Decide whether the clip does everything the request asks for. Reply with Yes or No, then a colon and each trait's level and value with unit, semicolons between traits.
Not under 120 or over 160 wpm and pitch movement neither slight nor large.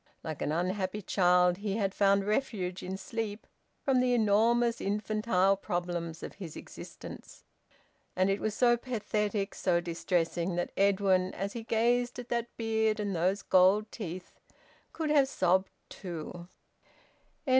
Yes: average, 140 wpm; average, 3.5 semitones